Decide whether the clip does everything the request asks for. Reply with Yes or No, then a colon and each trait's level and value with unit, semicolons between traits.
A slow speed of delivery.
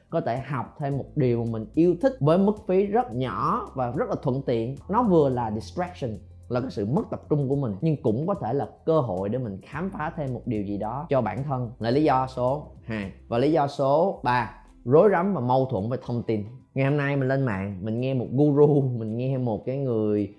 No: average, 245 wpm